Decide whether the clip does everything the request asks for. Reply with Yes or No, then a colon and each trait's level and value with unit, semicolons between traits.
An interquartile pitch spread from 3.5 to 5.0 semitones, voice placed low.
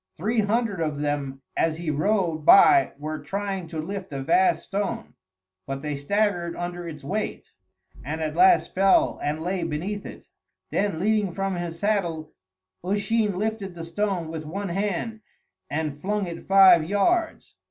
No: average, 4.4 semitones; medium, 180 Hz